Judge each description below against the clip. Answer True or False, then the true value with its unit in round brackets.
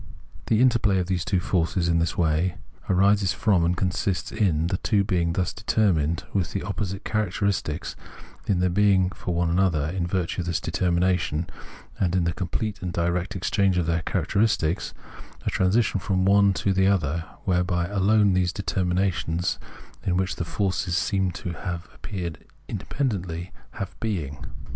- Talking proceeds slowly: False (155 wpm)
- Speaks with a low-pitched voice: True (90 Hz)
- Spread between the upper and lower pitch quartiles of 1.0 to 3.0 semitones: True (2.5 semitones)